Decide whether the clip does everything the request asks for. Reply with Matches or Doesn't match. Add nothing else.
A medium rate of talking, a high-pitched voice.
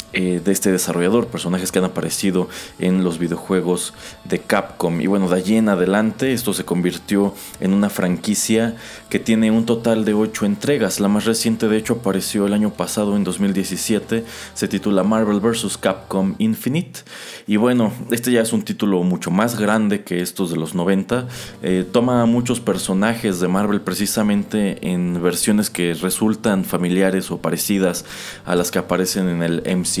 Doesn't match